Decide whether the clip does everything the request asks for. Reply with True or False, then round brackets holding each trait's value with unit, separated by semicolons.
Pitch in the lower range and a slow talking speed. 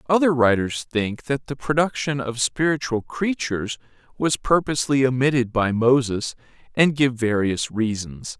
True (130 Hz; 130 wpm)